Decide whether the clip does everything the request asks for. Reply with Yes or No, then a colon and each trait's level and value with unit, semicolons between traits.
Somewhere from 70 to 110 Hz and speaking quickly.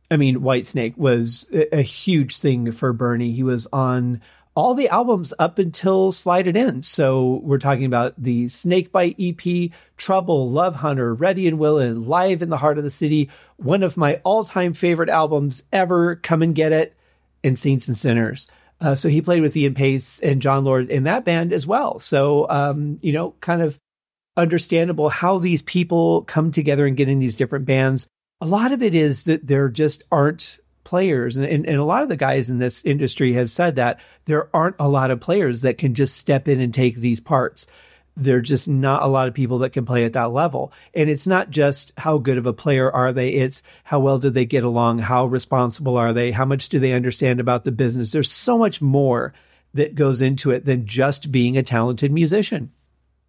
No: medium, 140 Hz; fast, 210 wpm